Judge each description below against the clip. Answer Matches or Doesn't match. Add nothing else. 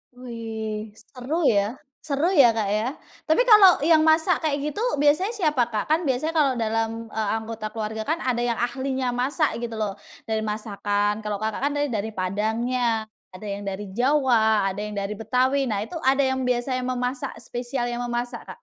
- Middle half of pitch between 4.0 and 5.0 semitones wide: Matches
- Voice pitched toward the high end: Matches